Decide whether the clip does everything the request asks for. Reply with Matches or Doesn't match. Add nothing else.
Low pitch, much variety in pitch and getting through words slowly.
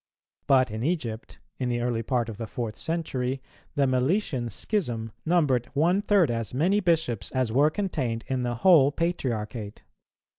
Doesn't match